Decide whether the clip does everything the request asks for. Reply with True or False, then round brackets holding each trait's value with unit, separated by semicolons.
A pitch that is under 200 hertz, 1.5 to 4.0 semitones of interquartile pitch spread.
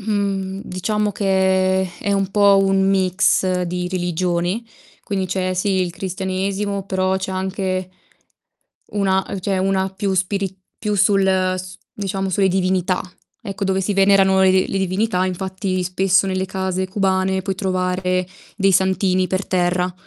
False (190 Hz; 0.9 semitones)